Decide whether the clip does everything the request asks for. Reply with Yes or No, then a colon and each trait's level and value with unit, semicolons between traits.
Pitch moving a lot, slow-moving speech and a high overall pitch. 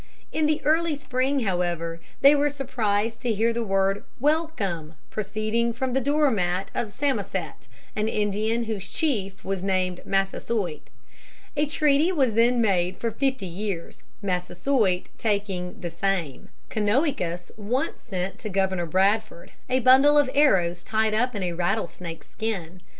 No: wide, 5.7 semitones; average, 145 wpm; high, 215 Hz